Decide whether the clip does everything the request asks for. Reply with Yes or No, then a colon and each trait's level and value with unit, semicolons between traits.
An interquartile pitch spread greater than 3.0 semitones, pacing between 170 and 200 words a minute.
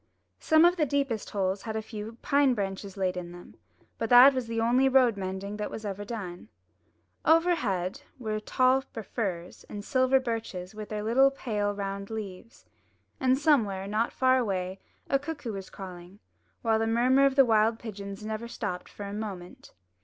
Yes: average, 4.5 semitones; average, 180 wpm